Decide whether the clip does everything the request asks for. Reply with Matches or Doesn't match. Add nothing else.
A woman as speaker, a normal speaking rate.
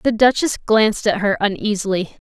Matches